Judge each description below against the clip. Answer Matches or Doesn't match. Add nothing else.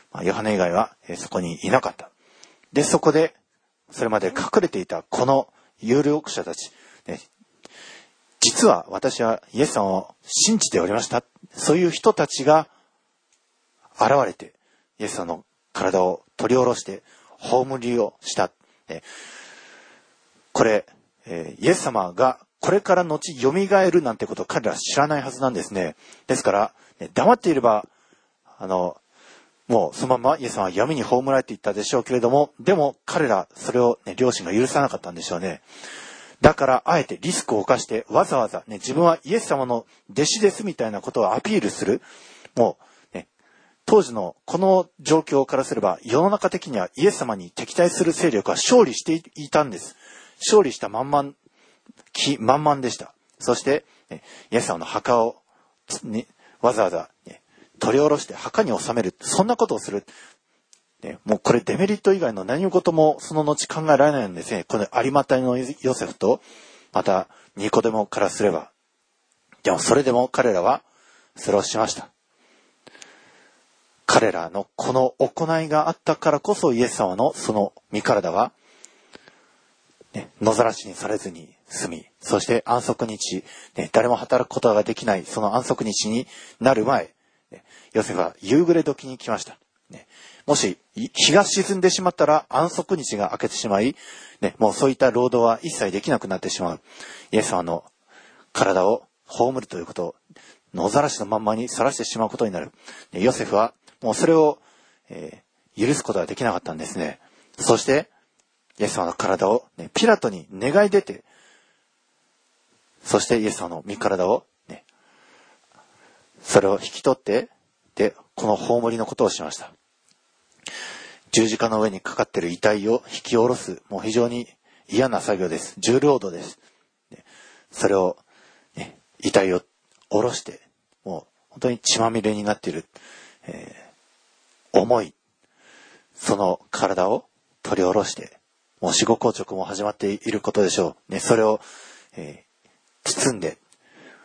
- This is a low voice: Matches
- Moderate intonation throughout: Doesn't match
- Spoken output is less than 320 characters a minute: Matches